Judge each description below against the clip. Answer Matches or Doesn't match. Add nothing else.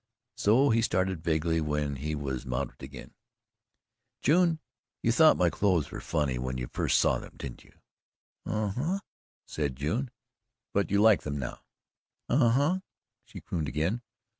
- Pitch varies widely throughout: Matches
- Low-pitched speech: Matches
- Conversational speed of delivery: Matches